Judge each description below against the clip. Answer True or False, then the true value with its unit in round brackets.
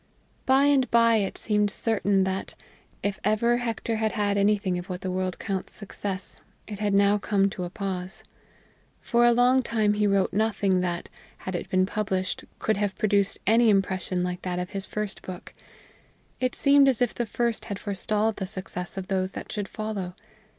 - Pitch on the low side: False (205 Hz)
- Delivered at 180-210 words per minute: True (185 wpm)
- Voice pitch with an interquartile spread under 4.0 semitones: True (2.7 semitones)